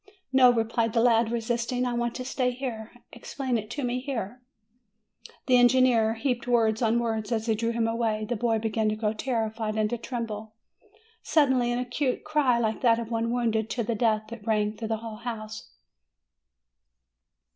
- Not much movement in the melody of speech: Yes, narrow, 1.9 semitones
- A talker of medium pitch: No, high, 230 Hz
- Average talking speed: Yes, average, 180 wpm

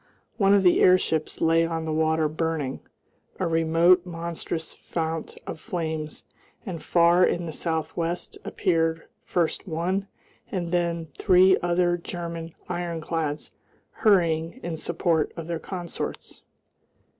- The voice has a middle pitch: Yes, medium, 170 Hz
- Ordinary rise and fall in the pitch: No, narrow, 1.5 semitones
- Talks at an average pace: No, slow, 125 wpm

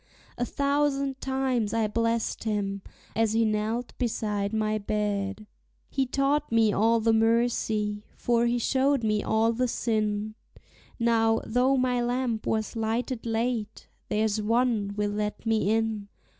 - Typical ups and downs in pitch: No, narrow, 2.3 semitones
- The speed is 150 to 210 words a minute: No, average, 140 wpm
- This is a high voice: Yes, high, 225 Hz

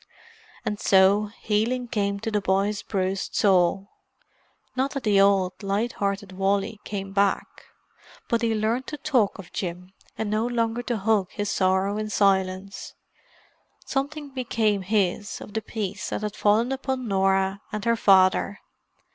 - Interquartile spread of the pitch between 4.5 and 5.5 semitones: No, narrow, 2.6 semitones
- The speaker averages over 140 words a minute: Yes, average, 150 wpm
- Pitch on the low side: No, high, 205 Hz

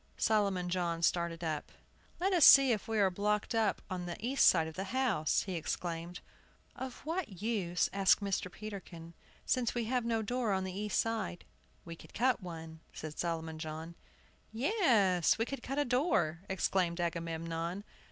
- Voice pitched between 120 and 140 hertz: No, high, 190 Hz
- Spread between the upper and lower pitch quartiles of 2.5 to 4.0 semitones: No, average, 5.2 semitones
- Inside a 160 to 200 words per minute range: Yes, average, 170 wpm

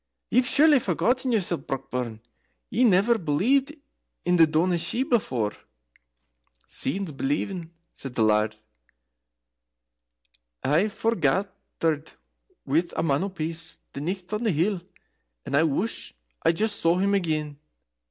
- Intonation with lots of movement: Yes, wide, 6.2 semitones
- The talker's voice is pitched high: No, medium, 170 Hz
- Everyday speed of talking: No, slow, 125 wpm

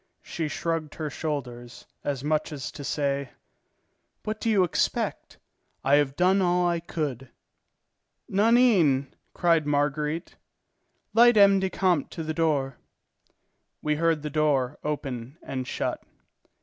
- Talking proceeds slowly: Yes, slow, 130 wpm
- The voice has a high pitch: No, medium, 155 Hz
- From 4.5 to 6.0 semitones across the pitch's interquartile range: No, average, 3.9 semitones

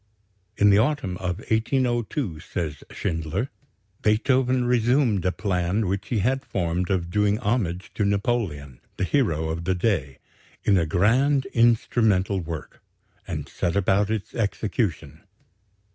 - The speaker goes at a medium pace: No, slow, 130 wpm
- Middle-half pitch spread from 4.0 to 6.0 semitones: Yes, average, 5.1 semitones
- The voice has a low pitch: Yes, low, 100 Hz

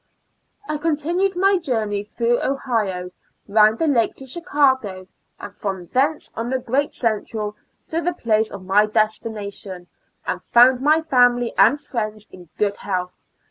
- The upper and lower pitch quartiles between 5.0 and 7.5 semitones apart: Yes, wide, 5.4 semitones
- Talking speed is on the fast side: No, average, 145 wpm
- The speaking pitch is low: No, high, 230 Hz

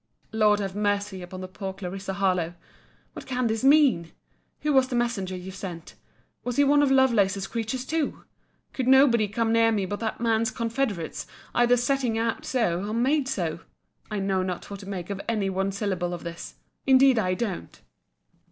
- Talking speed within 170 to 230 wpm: Yes, average, 175 wpm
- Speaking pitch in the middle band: No, high, 210 Hz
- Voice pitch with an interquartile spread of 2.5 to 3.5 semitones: No, average, 4.3 semitones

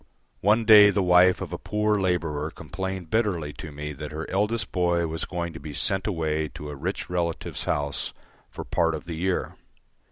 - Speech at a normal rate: Yes, average, 190 wpm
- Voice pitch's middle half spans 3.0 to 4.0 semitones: Yes, average, 3.6 semitones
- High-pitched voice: No, very low, 85 Hz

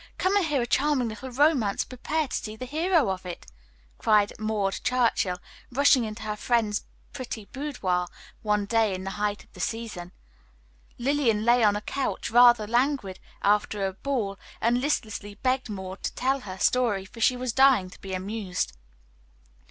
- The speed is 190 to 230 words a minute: No, average, 175 wpm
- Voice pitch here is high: Yes, high, 225 Hz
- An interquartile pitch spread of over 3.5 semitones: Yes, average, 4.2 semitones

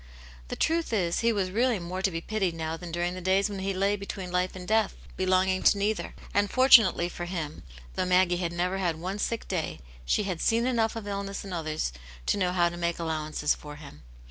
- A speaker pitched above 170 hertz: Yes, medium, 185 Hz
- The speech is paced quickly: Yes, fast, 220 wpm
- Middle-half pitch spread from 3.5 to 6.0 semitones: No, average, 2.8 semitones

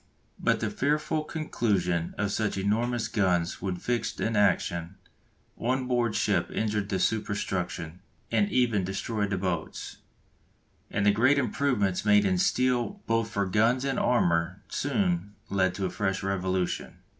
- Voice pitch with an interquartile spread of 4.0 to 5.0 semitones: Yes, average, 4.4 semitones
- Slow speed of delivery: No, average, 145 wpm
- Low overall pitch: Yes, low, 105 Hz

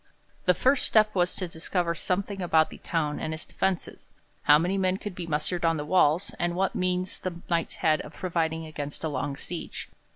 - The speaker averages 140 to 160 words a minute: No, average, 200 wpm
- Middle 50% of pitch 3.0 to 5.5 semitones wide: No, narrow, 2.6 semitones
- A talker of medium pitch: Yes, medium, 170 Hz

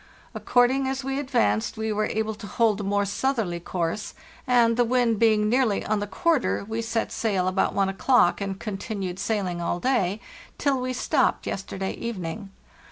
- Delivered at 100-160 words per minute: No, average, 170 wpm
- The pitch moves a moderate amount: Yes, average, 4.0 semitones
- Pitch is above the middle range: Yes, high, 215 Hz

